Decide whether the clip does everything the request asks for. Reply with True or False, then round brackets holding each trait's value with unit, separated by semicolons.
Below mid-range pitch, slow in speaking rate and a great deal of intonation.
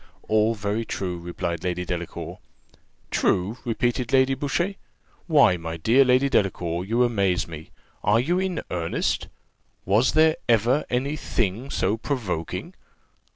True (110 Hz; 130 wpm; 6.6 semitones)